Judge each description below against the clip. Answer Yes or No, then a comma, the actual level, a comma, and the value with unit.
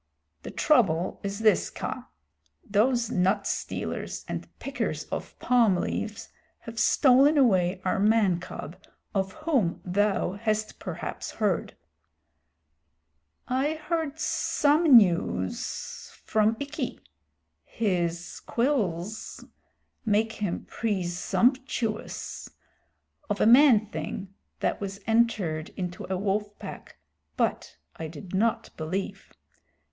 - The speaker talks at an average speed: No, slow, 105 wpm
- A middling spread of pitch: Yes, average, 4.6 semitones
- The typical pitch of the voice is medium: No, high, 210 Hz